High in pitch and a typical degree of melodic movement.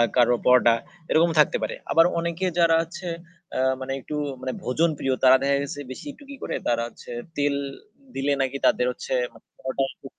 No: medium, 140 Hz; average, 4.2 semitones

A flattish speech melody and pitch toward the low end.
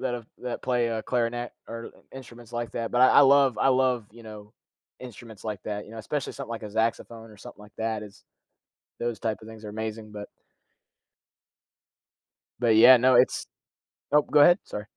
Yes: narrow, 2.3 semitones; low, 115 Hz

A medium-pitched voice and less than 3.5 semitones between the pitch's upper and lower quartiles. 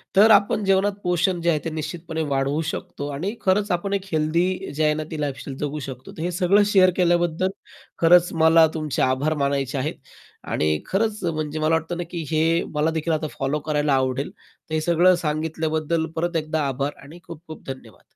Yes: medium, 160 Hz; average, 2.8 semitones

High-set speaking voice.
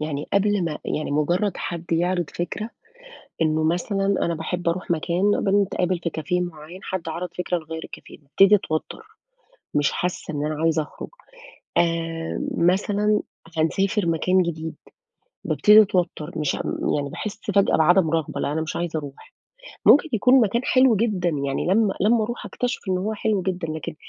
No: medium, 175 Hz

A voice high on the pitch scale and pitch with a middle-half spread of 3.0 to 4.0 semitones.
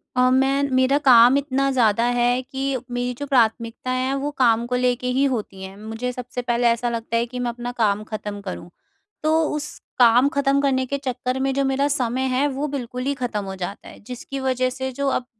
No: very high, 250 Hz; narrow, 2.5 semitones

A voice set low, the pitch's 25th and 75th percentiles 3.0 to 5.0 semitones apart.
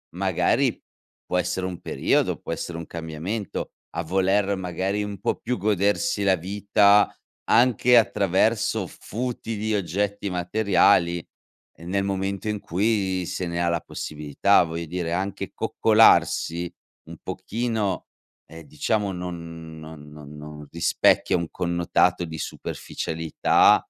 Yes: very low, 95 Hz; average, 3.4 semitones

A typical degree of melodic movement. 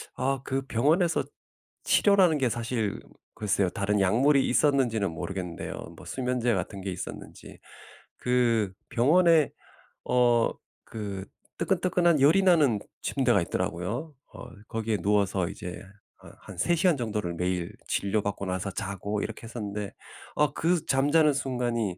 No: wide, 6.1 semitones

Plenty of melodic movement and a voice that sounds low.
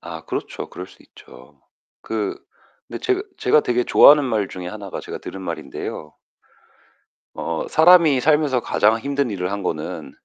Yes: wide, 7.7 semitones; low, 115 Hz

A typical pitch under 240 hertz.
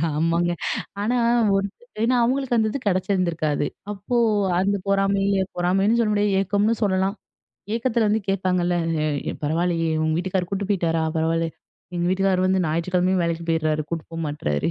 Yes: medium, 185 Hz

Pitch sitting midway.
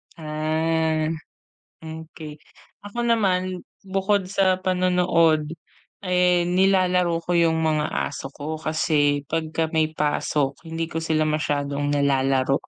Yes: medium, 160 Hz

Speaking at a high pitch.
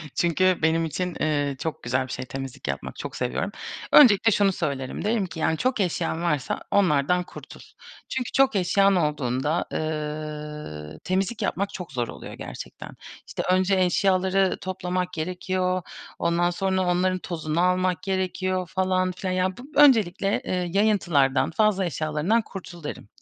No: medium, 180 Hz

